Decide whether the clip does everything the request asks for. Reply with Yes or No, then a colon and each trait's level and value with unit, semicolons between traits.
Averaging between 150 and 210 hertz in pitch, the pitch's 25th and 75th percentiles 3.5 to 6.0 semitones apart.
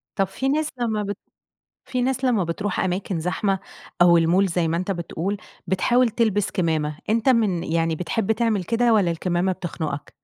Yes: high, 190 Hz; average, 4.7 semitones